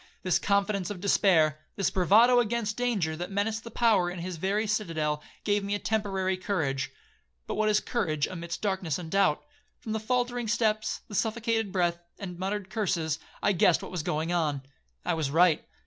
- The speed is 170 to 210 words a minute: Yes, average, 180 wpm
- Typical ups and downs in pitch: Yes, average, 4.0 semitones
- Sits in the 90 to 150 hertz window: No, high, 195 Hz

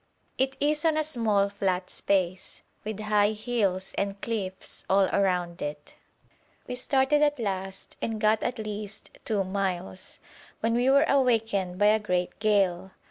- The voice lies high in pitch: Yes, high, 205 Hz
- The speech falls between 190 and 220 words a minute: No, average, 150 wpm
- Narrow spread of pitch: No, average, 3.7 semitones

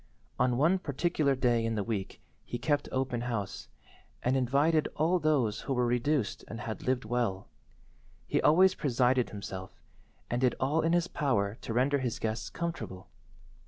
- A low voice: Yes, low, 125 Hz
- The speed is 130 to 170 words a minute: Yes, average, 160 wpm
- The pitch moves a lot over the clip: No, average, 4.4 semitones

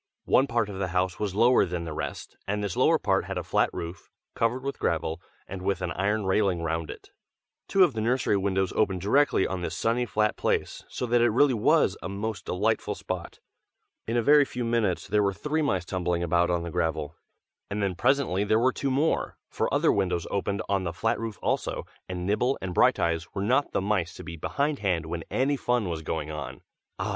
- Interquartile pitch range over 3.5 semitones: Yes, average, 5.0 semitones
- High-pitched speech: No, low, 100 Hz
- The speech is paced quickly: Yes, fast, 215 wpm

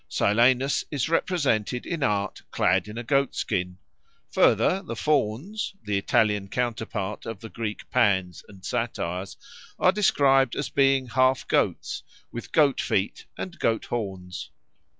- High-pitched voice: No, low, 115 Hz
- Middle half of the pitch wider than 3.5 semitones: Yes, average, 5.2 semitones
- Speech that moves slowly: Yes, slow, 130 wpm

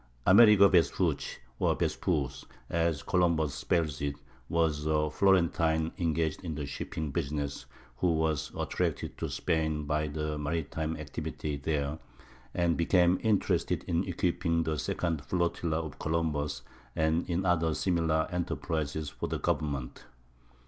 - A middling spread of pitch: No, narrow, 2.2 semitones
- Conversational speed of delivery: No, slow, 130 wpm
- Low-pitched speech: Yes, very low, 80 Hz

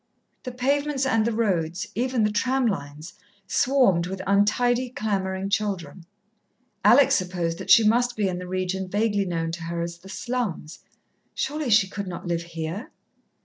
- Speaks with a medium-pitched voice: No, high, 195 Hz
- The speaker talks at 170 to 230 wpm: No, average, 160 wpm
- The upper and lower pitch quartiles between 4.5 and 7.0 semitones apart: Yes, wide, 5.6 semitones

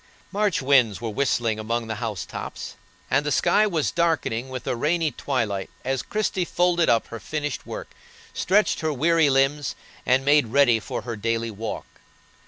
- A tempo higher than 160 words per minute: Yes, average, 170 wpm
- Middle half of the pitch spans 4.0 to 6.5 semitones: Yes, wide, 5.5 semitones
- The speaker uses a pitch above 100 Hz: Yes, low, 135 Hz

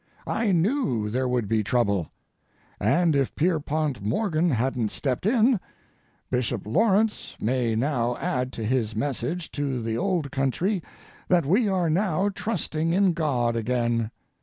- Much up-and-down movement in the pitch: Yes, wide, 7.1 semitones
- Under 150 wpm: Yes, slow, 135 wpm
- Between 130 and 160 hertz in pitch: Yes, medium, 140 Hz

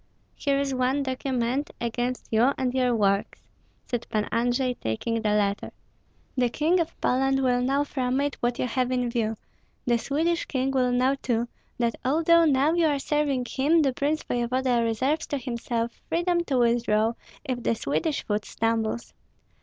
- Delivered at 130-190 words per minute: Yes, average, 170 wpm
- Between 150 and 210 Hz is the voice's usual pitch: No, very high, 255 Hz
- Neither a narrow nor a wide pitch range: Yes, average, 3.1 semitones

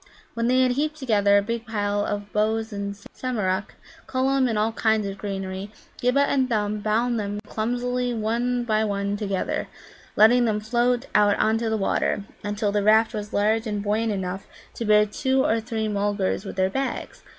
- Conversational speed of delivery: Yes, average, 185 wpm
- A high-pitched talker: Yes, high, 215 Hz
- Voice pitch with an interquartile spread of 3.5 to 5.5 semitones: No, average, 2.7 semitones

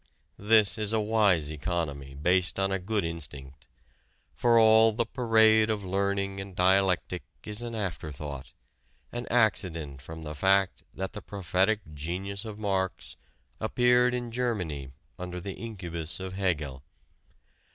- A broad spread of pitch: No, average, 4.6 semitones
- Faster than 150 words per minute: No, average, 140 wpm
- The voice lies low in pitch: Yes, very low, 95 Hz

